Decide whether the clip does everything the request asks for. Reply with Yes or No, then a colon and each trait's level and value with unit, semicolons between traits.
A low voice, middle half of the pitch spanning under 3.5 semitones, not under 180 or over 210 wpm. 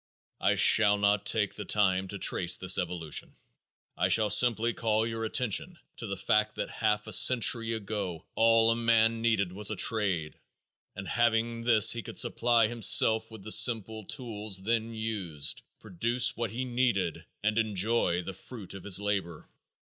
No: low, 110 Hz; average, 2.8 semitones; average, 165 wpm